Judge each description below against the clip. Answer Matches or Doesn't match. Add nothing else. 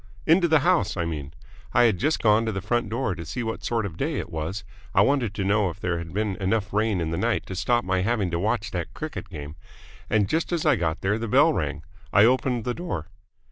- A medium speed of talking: Doesn't match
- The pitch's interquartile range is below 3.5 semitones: Doesn't match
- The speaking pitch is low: Matches